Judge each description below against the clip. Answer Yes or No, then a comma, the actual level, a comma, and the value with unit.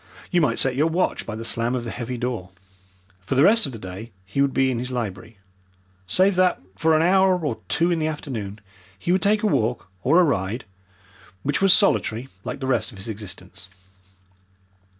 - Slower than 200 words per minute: No, fast, 205 wpm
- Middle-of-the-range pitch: No, low, 130 Hz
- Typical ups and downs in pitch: No, wide, 6.8 semitones